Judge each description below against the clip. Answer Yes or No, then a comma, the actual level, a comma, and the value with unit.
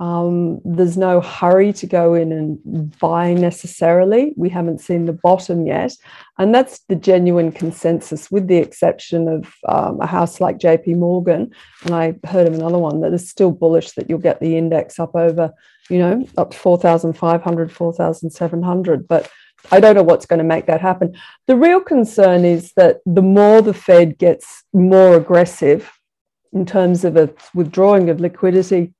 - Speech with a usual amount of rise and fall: No, narrow, 1.9 semitones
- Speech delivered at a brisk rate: No, average, 170 wpm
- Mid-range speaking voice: Yes, medium, 175 Hz